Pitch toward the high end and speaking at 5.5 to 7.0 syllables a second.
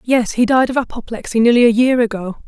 Yes: high, 235 Hz; 6.1 syllables/s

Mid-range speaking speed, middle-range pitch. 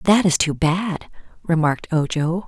Yes: average, 145 wpm; medium, 170 Hz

